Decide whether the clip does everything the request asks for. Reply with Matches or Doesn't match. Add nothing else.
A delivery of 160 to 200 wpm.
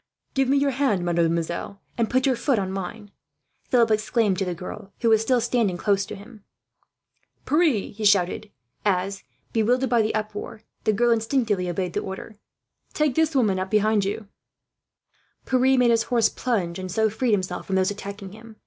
Matches